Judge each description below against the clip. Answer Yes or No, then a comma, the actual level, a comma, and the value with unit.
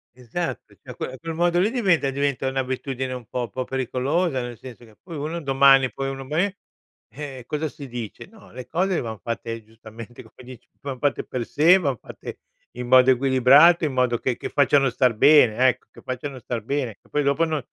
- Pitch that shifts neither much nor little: Yes, average, 3.2 semitones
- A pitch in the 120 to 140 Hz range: Yes, low, 135 Hz